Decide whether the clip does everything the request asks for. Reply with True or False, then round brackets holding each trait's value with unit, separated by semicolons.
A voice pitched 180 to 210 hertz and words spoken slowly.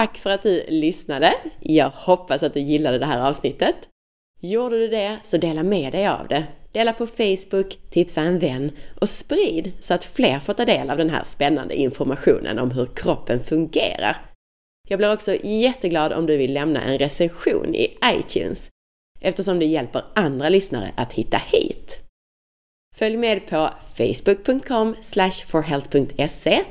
False (185 Hz; 155 wpm)